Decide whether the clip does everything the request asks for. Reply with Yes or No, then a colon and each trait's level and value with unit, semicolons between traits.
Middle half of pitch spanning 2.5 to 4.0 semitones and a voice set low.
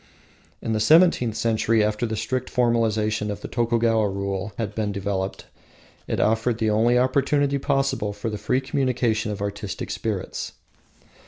Yes: average, 2.8 semitones; low, 110 Hz